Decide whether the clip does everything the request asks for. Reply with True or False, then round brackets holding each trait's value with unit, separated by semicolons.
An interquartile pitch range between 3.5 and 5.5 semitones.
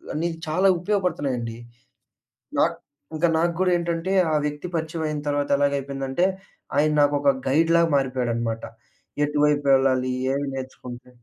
True (3.8 semitones)